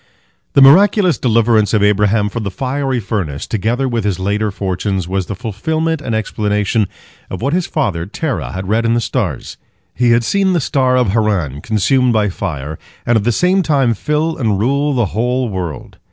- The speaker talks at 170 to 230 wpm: Yes, average, 185 wpm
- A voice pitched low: Yes, low, 115 Hz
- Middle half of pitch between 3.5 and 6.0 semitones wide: Yes, average, 4.9 semitones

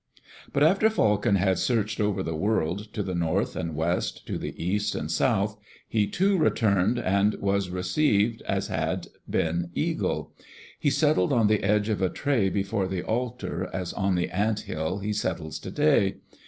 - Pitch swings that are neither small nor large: Yes, average, 3.4 semitones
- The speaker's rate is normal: Yes, average, 170 wpm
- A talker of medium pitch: No, low, 100 Hz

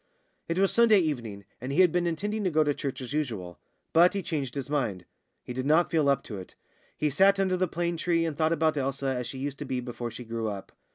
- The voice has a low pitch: No, medium, 145 Hz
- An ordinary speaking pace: No, fast, 250 wpm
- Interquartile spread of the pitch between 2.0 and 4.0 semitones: No, wide, 5.5 semitones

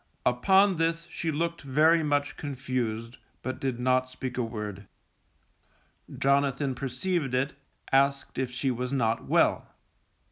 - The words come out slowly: Yes, slow, 130 wpm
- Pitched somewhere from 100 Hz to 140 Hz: Yes, low, 135 Hz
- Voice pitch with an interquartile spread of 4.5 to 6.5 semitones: No, average, 2.9 semitones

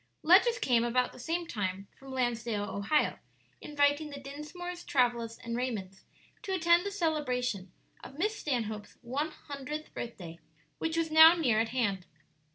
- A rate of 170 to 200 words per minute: No, average, 150 wpm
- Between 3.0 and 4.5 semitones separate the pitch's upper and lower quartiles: No, wide, 5.6 semitones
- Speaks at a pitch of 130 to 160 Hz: No, very high, 265 Hz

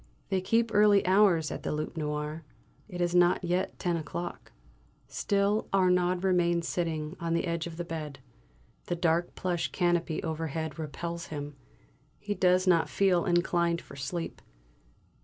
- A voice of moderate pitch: Yes, medium, 175 Hz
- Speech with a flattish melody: Yes, narrow, 2.1 semitones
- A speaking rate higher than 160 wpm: No, average, 150 wpm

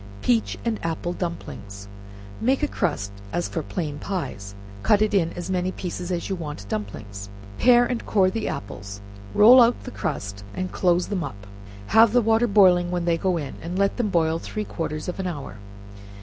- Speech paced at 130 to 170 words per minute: No, average, 185 wpm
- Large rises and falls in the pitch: Yes, wide, 6.0 semitones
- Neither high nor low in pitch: Yes, medium, 175 Hz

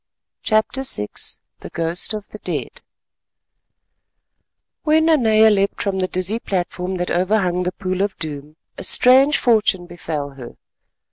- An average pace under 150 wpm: Yes, slow, 135 wpm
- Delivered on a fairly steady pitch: No, average, 3.9 semitones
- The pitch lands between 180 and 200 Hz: Yes, high, 190 Hz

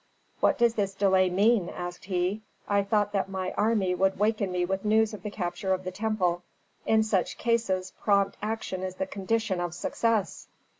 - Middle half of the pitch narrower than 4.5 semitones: Yes, average, 2.7 semitones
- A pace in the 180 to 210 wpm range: Yes, average, 185 wpm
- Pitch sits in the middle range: No, high, 195 Hz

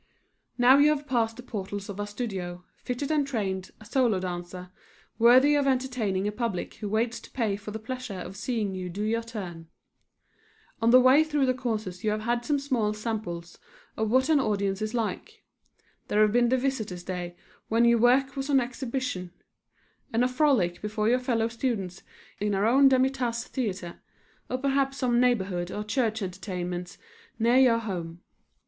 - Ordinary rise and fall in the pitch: Yes, average, 4.6 semitones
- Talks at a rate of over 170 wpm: Yes, average, 180 wpm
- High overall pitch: Yes, high, 225 Hz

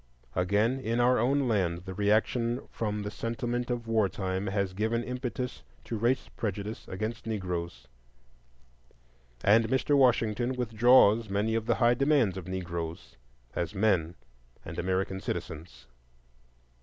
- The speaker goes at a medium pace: No, slow, 130 wpm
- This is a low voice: Yes, low, 110 Hz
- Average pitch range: Yes, average, 4.1 semitones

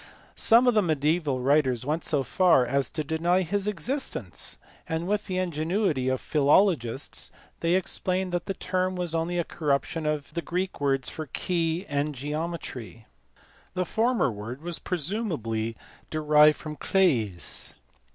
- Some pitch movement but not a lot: Yes, average, 4.7 semitones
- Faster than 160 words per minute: No, average, 140 wpm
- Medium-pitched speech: Yes, medium, 160 Hz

